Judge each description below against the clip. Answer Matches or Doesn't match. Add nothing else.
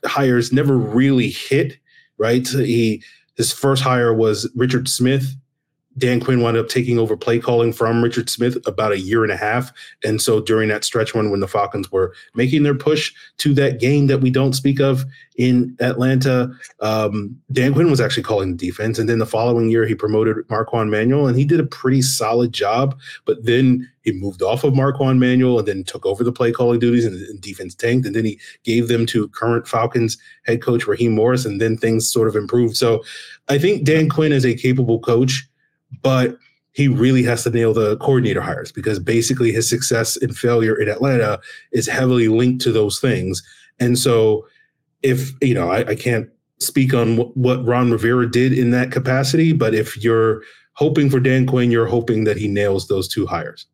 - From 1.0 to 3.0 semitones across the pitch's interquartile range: Matches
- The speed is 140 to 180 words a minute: Doesn't match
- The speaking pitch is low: Matches